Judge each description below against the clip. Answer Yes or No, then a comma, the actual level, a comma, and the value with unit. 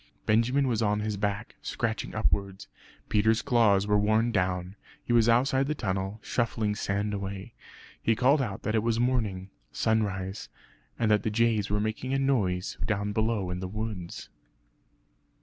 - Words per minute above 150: Yes, average, 160 wpm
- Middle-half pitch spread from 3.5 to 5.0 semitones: No, average, 2.7 semitones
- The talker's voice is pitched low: Yes, low, 105 Hz